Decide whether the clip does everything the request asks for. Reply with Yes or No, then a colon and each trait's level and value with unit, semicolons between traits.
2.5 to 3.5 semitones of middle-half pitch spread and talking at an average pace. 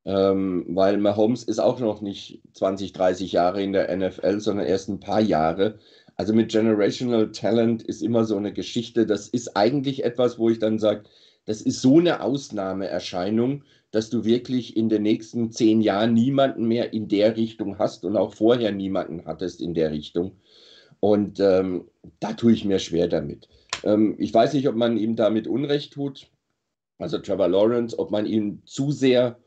Yes: average, 3.2 semitones; average, 180 wpm